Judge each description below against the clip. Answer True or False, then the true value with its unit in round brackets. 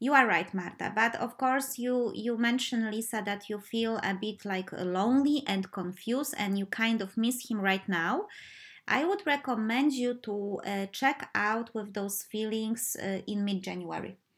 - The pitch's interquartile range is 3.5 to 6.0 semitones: True (3.9 semitones)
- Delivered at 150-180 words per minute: True (175 wpm)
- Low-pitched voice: False (220 Hz)